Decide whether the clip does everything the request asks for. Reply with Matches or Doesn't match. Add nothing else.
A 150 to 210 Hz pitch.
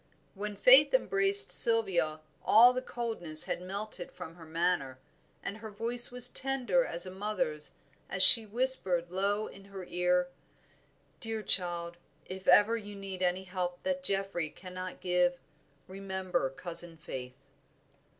Matches